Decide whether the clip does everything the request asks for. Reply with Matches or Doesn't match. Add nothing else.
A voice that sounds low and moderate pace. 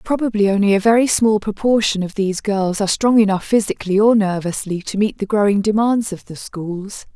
Doesn't match